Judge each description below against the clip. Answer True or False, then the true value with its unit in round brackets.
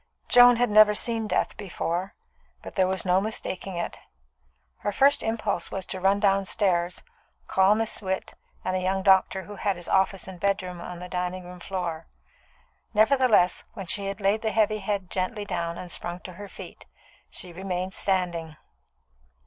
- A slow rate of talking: False (170 wpm)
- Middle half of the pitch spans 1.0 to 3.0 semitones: True (2.4 semitones)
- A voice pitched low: False (190 Hz)